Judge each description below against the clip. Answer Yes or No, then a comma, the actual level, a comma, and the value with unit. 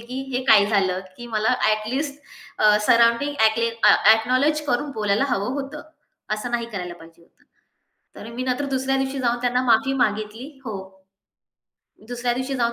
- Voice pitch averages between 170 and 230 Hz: No, high, 240 Hz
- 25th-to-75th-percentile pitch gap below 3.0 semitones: No, average, 3.3 semitones